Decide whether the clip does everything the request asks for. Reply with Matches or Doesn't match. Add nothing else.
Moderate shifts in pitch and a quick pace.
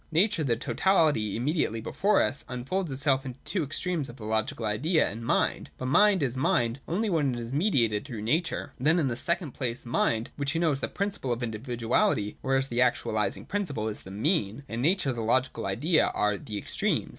Doesn't match